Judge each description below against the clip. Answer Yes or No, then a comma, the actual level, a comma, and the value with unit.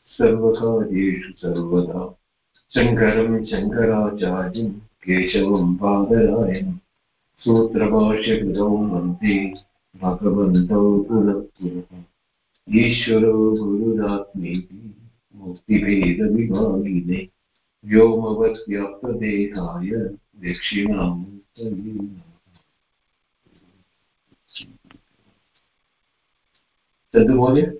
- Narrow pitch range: No, average, 3.3 semitones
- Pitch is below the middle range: Yes, low, 100 Hz